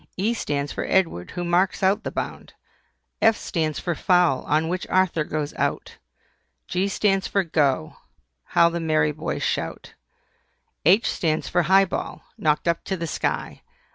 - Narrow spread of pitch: No, average, 3.5 semitones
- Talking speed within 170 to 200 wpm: No, average, 160 wpm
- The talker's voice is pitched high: No, medium, 170 Hz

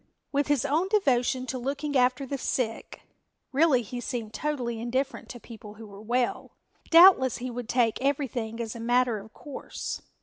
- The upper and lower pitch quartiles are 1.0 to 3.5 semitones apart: Yes, average, 3.1 semitones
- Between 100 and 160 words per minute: No, average, 170 wpm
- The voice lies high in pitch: Yes, very high, 250 Hz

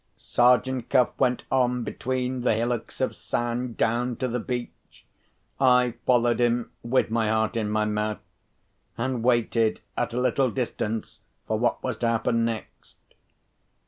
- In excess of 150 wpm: No, average, 145 wpm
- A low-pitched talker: Yes, low, 120 Hz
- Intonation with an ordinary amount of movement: No, narrow, 1.6 semitones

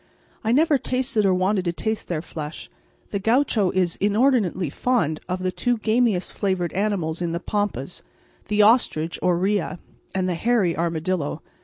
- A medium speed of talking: Yes, average, 160 wpm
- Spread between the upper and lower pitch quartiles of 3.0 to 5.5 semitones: Yes, average, 4.2 semitones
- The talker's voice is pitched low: No, high, 190 Hz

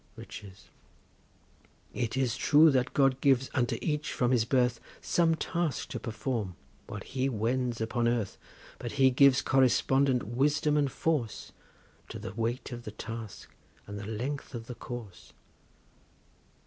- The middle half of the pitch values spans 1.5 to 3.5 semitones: Yes, average, 3.0 semitones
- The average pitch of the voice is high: No, low, 125 Hz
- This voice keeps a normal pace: Yes, average, 145 wpm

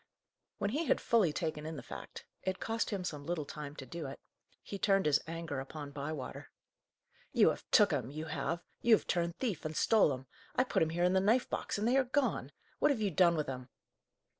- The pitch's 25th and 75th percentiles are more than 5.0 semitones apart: Yes, wide, 5.4 semitones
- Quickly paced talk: Yes, fast, 225 wpm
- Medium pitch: Yes, medium, 170 Hz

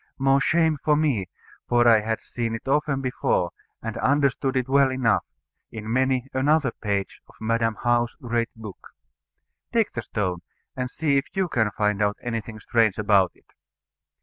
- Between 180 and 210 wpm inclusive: No, average, 165 wpm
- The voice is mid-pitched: No, low, 120 Hz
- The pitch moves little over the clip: No, average, 3.8 semitones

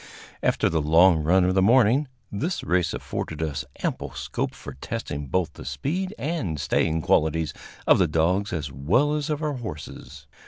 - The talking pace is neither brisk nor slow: Yes, average, 170 wpm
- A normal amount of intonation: No, wide, 9.0 semitones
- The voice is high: No, very low, 90 Hz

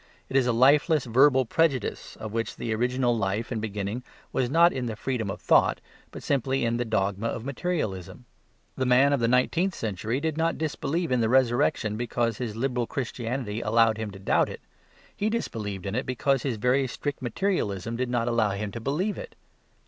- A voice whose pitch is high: No, low, 120 Hz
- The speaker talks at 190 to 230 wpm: Yes, average, 195 wpm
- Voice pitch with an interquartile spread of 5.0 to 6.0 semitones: No, average, 3.7 semitones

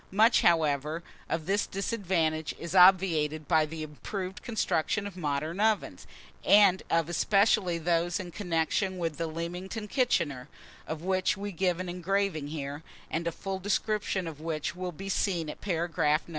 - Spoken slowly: No, average, 155 wpm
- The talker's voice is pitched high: No, medium, 175 Hz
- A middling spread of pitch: Yes, average, 3.4 semitones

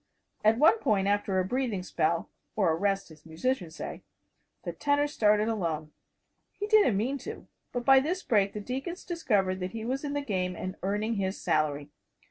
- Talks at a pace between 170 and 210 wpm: Yes, average, 185 wpm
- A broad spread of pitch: Yes, wide, 6.2 semitones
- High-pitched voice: Yes, high, 210 Hz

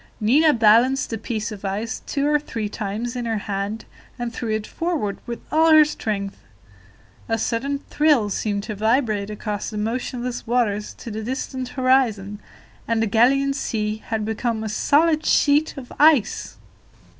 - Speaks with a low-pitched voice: No, high, 230 Hz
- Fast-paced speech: No, average, 160 wpm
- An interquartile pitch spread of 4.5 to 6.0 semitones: No, average, 4.1 semitones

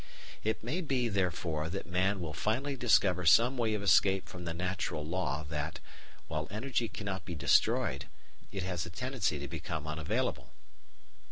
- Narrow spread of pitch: No, wide, 5.4 semitones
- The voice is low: Yes, very low, 90 Hz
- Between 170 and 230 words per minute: No, average, 160 wpm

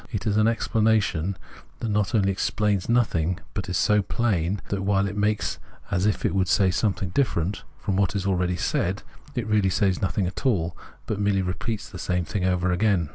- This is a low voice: Yes, low, 100 Hz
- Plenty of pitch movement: No, narrow, 2.6 semitones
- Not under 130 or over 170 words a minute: No, average, 195 wpm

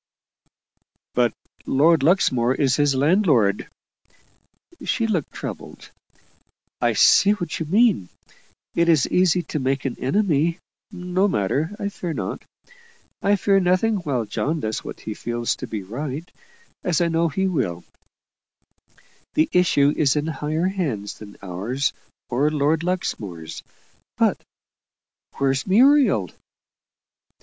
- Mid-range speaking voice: Yes, medium, 155 Hz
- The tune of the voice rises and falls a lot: Yes, wide, 5.9 semitones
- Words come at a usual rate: No, slow, 125 wpm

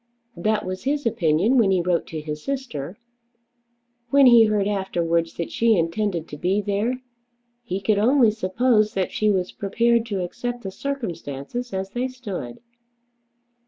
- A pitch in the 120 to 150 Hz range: No, high, 205 Hz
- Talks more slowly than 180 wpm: Yes, average, 155 wpm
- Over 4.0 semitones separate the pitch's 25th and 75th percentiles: Yes, average, 5.0 semitones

